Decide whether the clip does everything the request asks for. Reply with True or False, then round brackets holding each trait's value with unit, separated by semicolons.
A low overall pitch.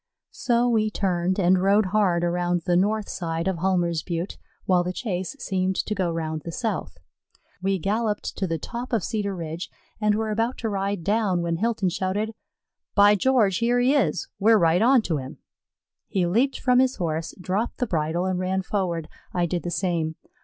False (190 Hz)